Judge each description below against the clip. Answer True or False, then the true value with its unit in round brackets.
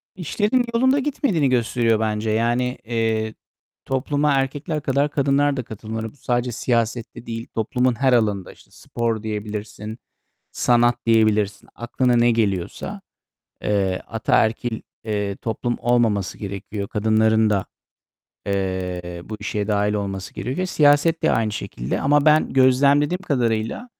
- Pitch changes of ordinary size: True (4.0 semitones)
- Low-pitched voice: True (115 Hz)